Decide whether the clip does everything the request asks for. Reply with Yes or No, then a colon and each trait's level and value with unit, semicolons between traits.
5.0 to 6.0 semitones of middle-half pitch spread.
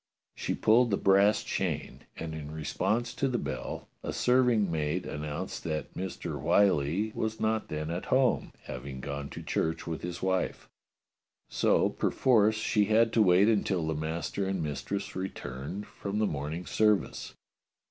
Yes: wide, 5.6 semitones